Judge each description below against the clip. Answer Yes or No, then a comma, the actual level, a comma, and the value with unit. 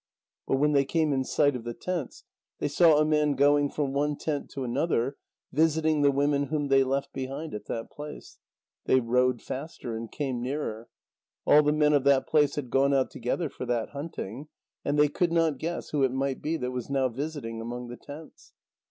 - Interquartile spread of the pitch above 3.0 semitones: No, average, 2.7 semitones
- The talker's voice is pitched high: No, medium, 140 Hz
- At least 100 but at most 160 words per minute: No, fast, 205 wpm